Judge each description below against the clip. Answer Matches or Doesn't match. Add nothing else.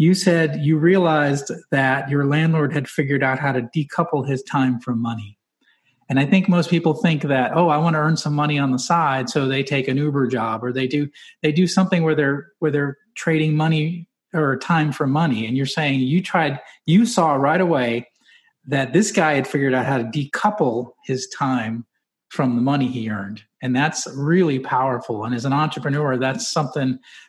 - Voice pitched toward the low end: Doesn't match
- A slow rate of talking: Doesn't match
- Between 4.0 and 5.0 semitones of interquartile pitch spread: Doesn't match